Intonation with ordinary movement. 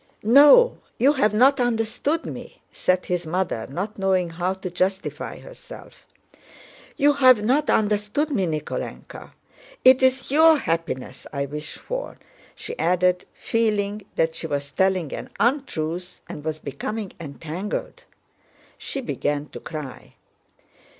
No: wide, 7.8 semitones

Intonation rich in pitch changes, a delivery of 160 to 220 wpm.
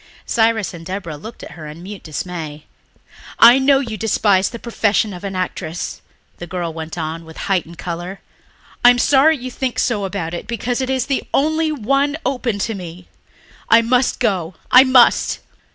Yes: wide, 6.2 semitones; average, 180 wpm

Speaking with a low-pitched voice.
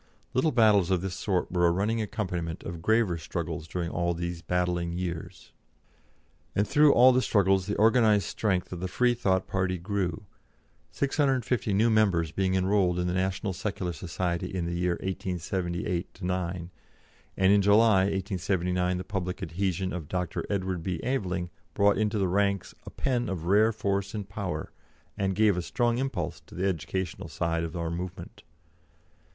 Yes: very low, 95 Hz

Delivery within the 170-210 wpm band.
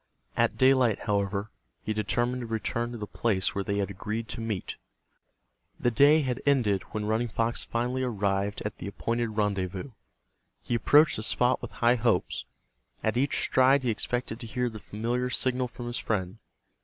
Yes: average, 175 wpm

